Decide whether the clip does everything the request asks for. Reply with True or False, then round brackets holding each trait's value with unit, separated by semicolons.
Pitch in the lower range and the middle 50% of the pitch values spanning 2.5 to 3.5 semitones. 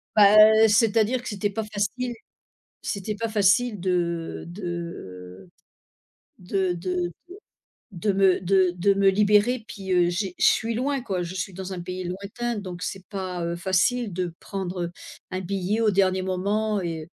False (190 Hz; 2.9 semitones)